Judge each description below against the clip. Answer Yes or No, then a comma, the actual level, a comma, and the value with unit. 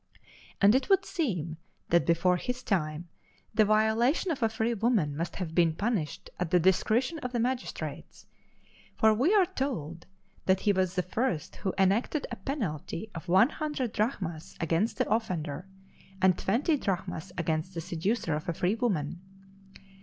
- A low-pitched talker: No, high, 195 Hz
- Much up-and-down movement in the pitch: Yes, wide, 5.9 semitones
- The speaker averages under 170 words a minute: Yes, average, 160 wpm